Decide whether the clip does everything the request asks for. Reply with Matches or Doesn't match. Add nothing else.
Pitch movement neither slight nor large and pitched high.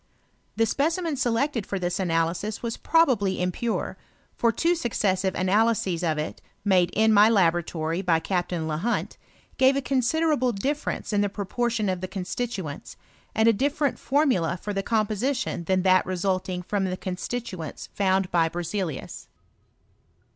Matches